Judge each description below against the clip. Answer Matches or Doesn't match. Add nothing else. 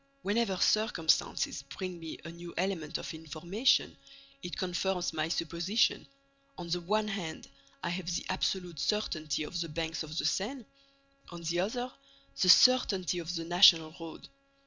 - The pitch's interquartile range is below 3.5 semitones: Matches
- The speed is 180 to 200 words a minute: Doesn't match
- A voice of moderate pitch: Matches